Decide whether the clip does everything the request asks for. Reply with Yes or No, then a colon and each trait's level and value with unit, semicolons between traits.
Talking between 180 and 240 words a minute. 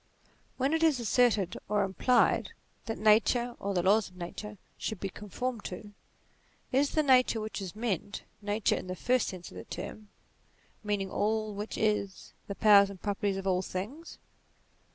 No: average, 170 wpm